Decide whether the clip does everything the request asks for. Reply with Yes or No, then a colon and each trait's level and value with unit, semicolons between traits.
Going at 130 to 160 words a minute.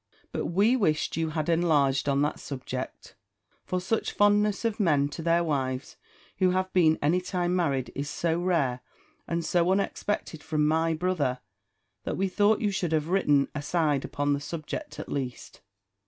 No: average, 170 wpm